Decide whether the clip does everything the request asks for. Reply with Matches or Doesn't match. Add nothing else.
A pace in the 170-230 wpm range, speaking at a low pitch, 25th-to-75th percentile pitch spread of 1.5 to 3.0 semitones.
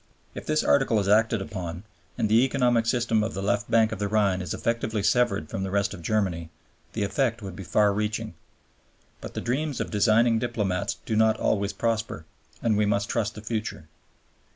Matches